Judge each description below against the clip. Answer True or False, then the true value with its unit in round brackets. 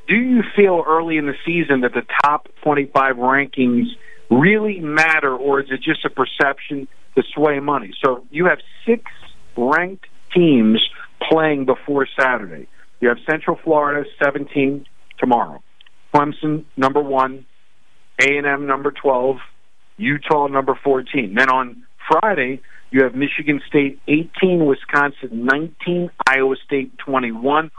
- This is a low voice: False (145 Hz)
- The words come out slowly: True (130 wpm)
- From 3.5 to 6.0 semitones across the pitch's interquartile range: False (2.8 semitones)